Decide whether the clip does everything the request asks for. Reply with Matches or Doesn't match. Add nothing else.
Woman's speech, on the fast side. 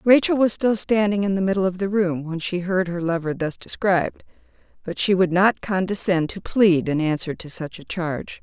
Matches